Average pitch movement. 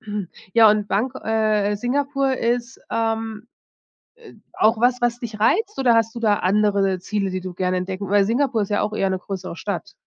Yes: average, 3.1 semitones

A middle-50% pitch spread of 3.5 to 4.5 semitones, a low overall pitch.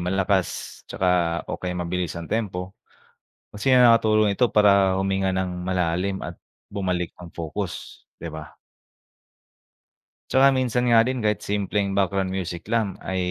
No: average, 3.0 semitones; very low, 95 Hz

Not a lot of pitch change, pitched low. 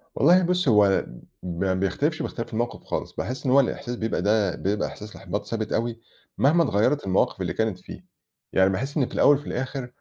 No: wide, 5.6 semitones; low, 115 Hz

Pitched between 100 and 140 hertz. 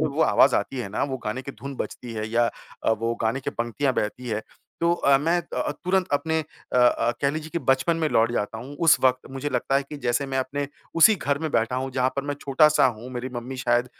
Yes: low, 135 Hz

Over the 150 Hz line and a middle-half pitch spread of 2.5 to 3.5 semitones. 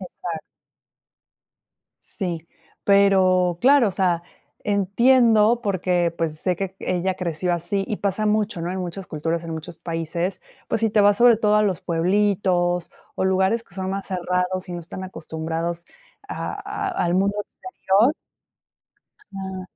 Yes: medium, 185 Hz; average, 2.8 semitones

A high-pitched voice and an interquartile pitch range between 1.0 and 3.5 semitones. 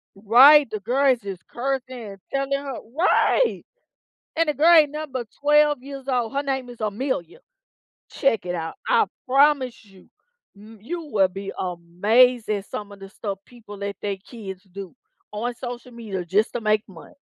No: high, 235 Hz; wide, 5.4 semitones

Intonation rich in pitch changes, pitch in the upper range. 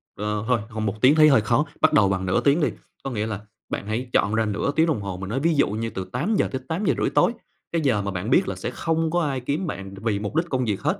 No: wide, 6.6 semitones; low, 120 Hz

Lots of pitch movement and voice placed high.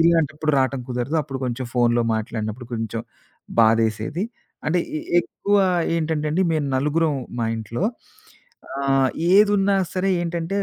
No: wide, 5.8 semitones; medium, 140 Hz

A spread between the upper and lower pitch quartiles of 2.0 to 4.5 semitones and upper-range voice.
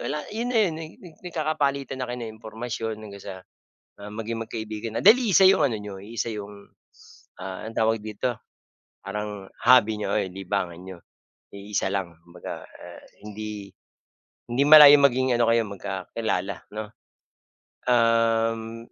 No: average, 3.8 semitones; low, 110 Hz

